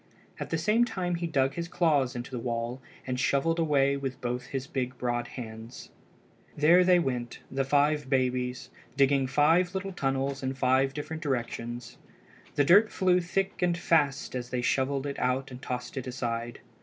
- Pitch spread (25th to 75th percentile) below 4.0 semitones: No, average, 4.3 semitones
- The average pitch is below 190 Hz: Yes, low, 135 Hz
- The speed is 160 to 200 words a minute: Yes, average, 170 wpm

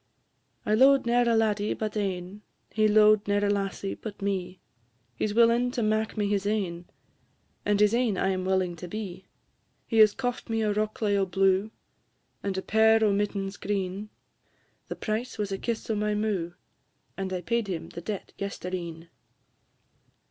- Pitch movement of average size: No, narrow, 2.3 semitones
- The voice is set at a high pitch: Yes, high, 205 Hz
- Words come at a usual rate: Yes, average, 175 wpm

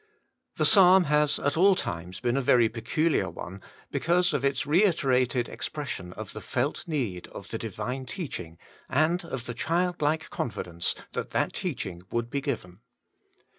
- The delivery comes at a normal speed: Yes, average, 155 wpm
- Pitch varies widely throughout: Yes, wide, 6.2 semitones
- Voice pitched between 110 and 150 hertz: Yes, low, 135 Hz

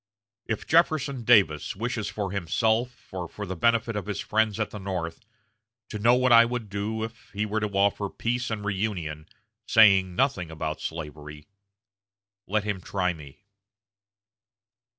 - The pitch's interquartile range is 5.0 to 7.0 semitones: No, average, 3.7 semitones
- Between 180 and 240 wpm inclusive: No, average, 150 wpm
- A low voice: Yes, low, 105 Hz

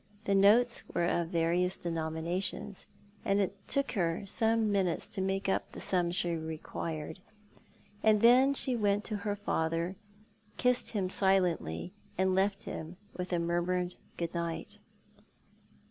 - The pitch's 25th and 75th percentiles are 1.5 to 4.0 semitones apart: Yes, average, 3.3 semitones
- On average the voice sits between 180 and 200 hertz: Yes, medium, 185 Hz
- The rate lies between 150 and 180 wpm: No, average, 140 wpm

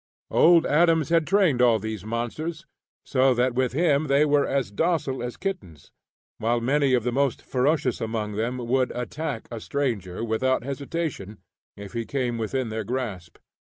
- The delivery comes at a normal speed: Yes, average, 160 wpm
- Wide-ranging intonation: No, average, 4.2 semitones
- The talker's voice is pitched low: Yes, low, 125 Hz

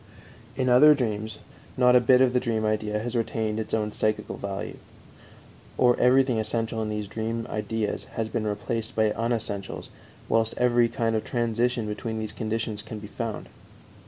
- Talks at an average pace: Yes, average, 165 wpm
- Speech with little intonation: Yes, narrow, 1.9 semitones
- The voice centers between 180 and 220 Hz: No, low, 110 Hz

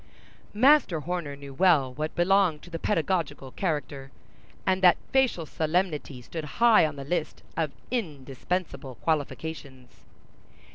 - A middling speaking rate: No, slow, 125 wpm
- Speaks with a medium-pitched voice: Yes, medium, 160 Hz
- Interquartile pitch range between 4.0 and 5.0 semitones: Yes, average, 4.5 semitones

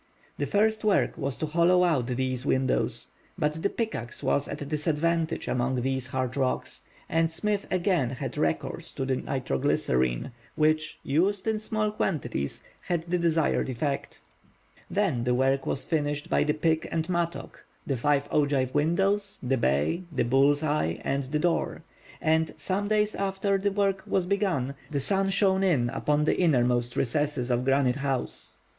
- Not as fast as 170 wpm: Yes, average, 160 wpm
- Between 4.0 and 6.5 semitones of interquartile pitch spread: Yes, wide, 5.5 semitones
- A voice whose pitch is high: No, medium, 150 Hz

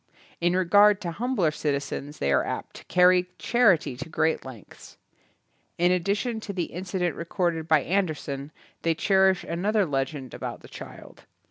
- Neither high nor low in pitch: Yes, medium, 175 Hz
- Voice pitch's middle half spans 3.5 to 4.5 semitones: Yes, average, 3.8 semitones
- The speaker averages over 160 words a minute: No, average, 155 wpm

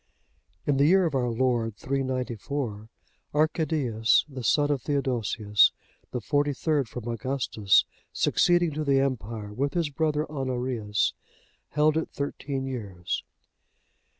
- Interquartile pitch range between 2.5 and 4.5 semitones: Yes, average, 4.1 semitones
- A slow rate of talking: Yes, slow, 125 wpm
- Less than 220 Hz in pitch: Yes, low, 135 Hz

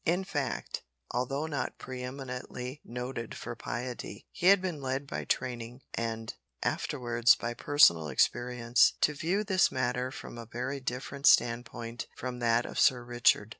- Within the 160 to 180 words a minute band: No, average, 150 wpm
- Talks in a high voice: No, low, 125 Hz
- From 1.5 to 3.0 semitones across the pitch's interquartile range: Yes, narrow, 2.6 semitones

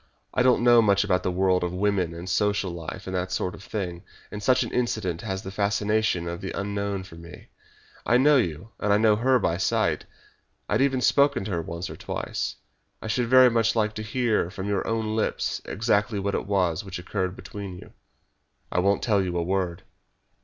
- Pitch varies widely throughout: No, average, 3.3 semitones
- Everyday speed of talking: No, fast, 210 wpm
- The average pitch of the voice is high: No, low, 100 Hz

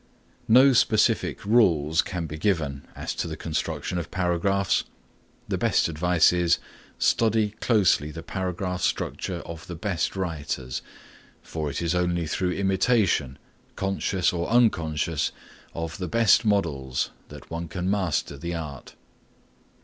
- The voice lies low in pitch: Yes, very low, 90 Hz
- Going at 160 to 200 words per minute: No, slow, 135 wpm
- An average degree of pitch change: Yes, average, 3.6 semitones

